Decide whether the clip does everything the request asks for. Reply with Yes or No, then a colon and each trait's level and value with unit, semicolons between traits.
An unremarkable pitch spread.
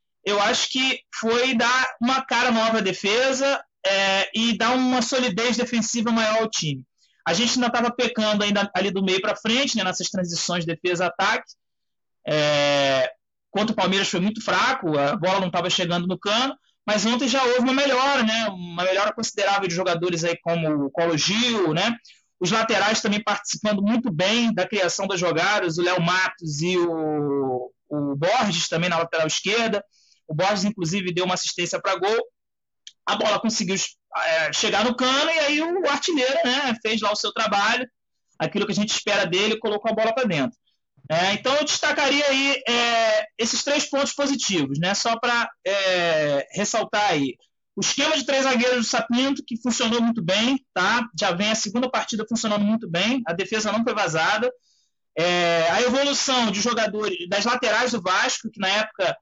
Yes: average, 4.9 semitones